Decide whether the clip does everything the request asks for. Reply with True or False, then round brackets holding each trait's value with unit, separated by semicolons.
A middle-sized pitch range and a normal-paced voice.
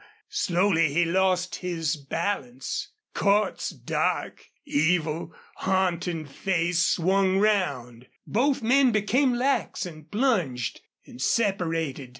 False (4.5 semitones; 100 wpm)